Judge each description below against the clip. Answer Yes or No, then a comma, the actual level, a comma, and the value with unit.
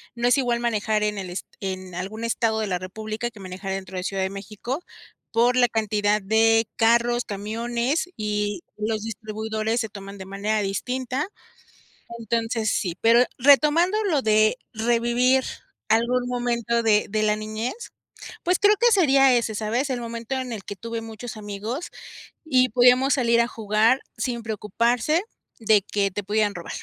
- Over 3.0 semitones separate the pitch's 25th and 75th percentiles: No, narrow, 2.6 semitones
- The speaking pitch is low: No, high, 225 Hz